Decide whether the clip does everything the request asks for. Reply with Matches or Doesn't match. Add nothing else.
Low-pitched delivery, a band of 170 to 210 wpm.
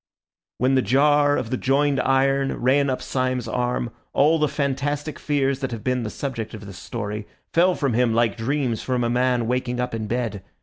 Matches